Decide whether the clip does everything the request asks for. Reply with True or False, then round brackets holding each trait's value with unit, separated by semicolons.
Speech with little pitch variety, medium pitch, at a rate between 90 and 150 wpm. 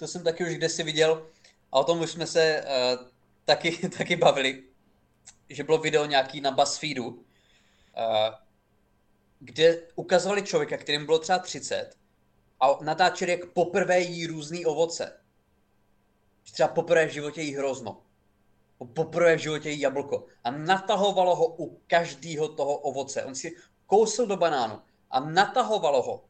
False (3.7 semitones; 160 Hz; 145 wpm)